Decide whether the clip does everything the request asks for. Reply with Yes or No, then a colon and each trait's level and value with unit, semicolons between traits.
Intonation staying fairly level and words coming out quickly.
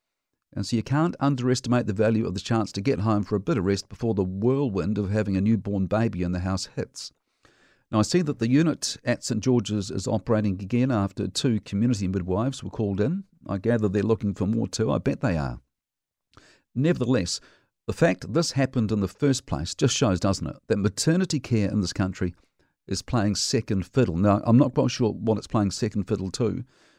No: average, 3.9 semitones; fast, 210 wpm